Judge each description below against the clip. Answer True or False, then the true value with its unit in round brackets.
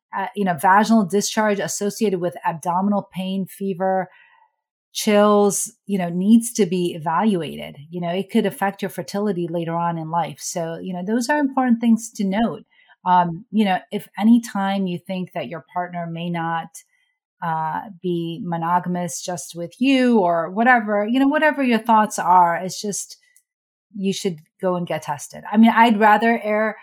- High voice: True (195 Hz)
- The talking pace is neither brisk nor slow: True (165 wpm)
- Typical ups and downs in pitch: True (4.0 semitones)